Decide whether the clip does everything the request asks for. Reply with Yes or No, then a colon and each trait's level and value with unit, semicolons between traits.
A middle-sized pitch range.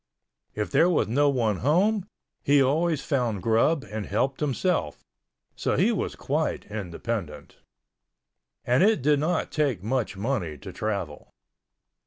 No: wide, 6.2 semitones